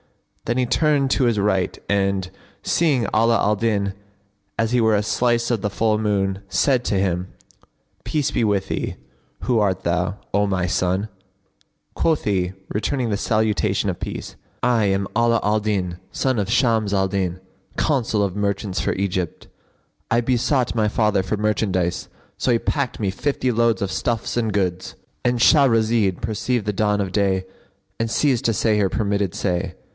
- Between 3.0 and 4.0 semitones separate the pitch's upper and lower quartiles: Yes, average, 3.3 semitones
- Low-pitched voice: Yes, low, 105 Hz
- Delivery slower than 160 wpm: No, average, 170 wpm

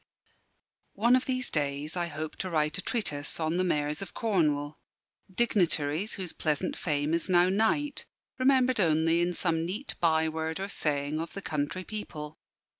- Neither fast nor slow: Yes, average, 165 wpm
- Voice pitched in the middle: Yes, medium, 170 Hz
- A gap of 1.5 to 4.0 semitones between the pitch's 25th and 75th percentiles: No, average, 4.5 semitones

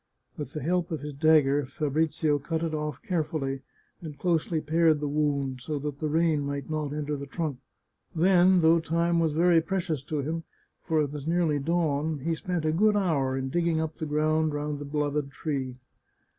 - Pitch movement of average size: No, narrow, 2.3 semitones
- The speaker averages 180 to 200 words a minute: Yes, average, 190 wpm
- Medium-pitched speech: Yes, medium, 155 Hz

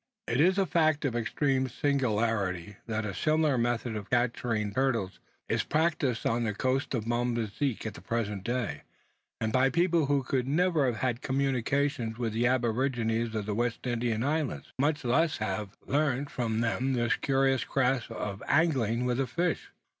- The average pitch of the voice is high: No, low, 125 Hz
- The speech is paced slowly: No, average, 175 wpm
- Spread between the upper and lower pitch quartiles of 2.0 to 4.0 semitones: Yes, average, 3.6 semitones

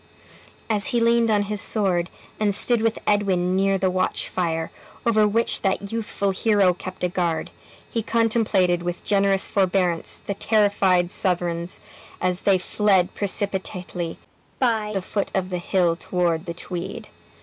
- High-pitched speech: Yes, high, 195 Hz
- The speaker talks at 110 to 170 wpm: Yes, average, 150 wpm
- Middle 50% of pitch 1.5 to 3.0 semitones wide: Yes, average, 2.7 semitones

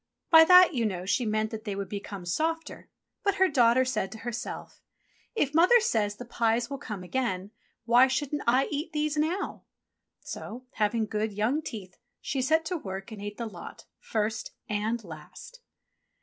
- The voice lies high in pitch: Yes, high, 235 Hz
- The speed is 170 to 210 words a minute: Yes, average, 175 wpm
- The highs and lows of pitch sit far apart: Yes, wide, 6.0 semitones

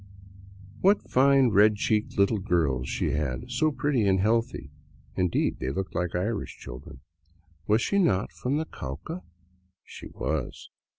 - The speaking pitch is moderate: No, low, 105 Hz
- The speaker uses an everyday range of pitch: No, wide, 6.5 semitones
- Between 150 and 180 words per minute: No, average, 140 wpm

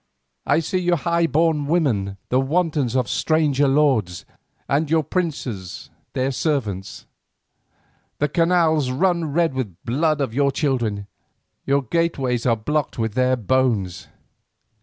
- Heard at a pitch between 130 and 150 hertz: Yes, medium, 140 Hz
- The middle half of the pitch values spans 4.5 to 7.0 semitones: Yes, average, 4.9 semitones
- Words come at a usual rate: No, slow, 130 wpm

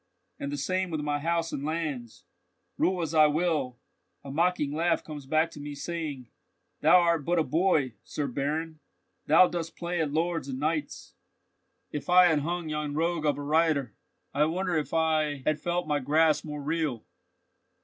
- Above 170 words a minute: Yes, average, 180 wpm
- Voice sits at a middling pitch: Yes, medium, 155 Hz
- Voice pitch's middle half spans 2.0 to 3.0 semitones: Yes, narrow, 2.5 semitones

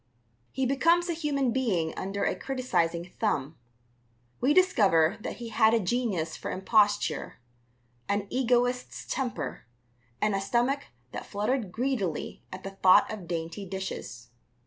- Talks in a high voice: Yes, high, 215 Hz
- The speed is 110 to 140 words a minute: Yes, slow, 135 wpm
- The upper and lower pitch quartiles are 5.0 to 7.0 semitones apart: Yes, wide, 5.6 semitones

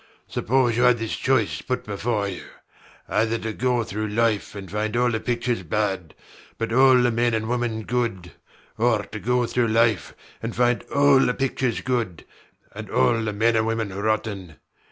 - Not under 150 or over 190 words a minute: Yes, average, 175 wpm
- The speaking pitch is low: Yes, low, 115 Hz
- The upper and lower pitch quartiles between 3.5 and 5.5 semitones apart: No, narrow, 2.4 semitones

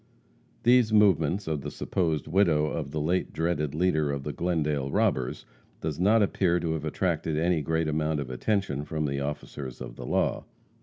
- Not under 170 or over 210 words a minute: Yes, average, 175 wpm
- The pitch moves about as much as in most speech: Yes, average, 3.2 semitones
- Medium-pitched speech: No, very low, 80 Hz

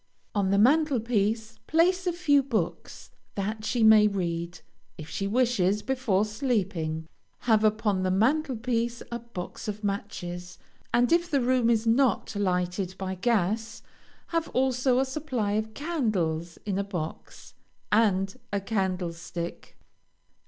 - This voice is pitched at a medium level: No, high, 215 Hz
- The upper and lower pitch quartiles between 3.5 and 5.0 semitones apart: Yes, average, 4.6 semitones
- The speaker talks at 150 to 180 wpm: No, average, 140 wpm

